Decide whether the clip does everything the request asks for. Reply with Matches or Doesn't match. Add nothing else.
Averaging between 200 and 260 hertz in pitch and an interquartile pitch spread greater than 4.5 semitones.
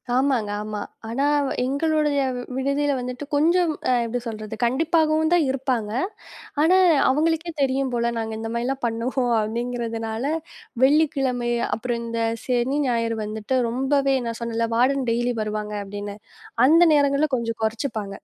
Doesn't match